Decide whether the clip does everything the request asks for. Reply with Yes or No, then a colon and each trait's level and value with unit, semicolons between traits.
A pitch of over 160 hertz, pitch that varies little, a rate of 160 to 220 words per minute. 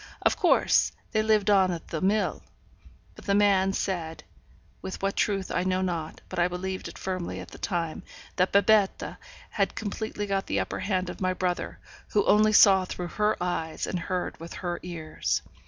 Yes: medium, 185 Hz; narrow, 2.2 semitones; average, 185 wpm